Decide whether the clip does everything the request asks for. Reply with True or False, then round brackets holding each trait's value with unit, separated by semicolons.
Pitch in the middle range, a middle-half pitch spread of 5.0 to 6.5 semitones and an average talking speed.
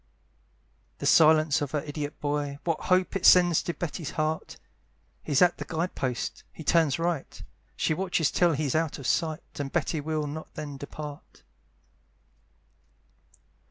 False (155 Hz; 2.4 semitones; 150 wpm)